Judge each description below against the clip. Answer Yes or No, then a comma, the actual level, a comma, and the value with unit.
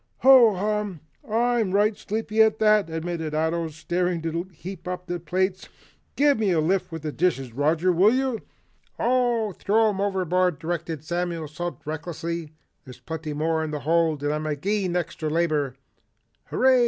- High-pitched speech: No, medium, 175 Hz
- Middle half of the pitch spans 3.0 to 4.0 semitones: No, average, 4.6 semitones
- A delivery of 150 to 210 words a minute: Yes, average, 160 wpm